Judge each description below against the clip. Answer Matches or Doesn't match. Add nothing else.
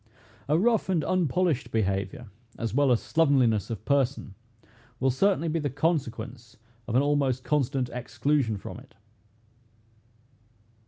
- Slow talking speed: Matches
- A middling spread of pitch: Matches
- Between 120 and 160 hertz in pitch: Matches